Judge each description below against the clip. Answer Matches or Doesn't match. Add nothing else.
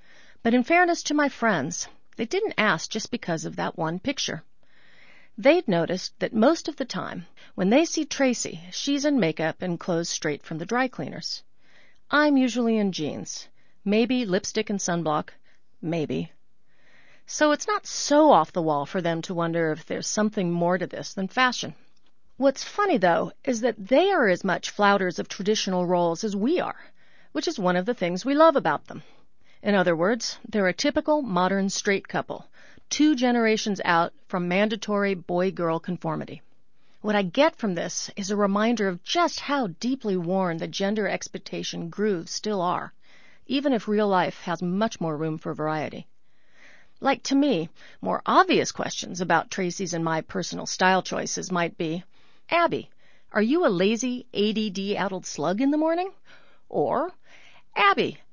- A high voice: Matches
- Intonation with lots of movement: Matches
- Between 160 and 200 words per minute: Matches